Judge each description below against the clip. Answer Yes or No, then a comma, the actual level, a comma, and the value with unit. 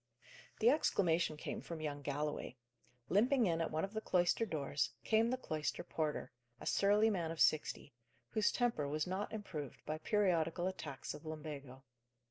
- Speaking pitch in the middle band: Yes, medium, 165 Hz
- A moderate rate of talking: Yes, average, 160 wpm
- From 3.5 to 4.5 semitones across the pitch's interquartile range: No, wide, 5.4 semitones